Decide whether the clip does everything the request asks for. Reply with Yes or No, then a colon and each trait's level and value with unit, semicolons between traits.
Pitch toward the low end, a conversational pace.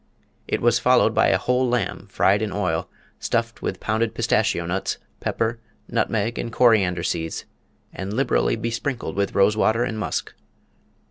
Yes: low, 110 Hz; average, 150 wpm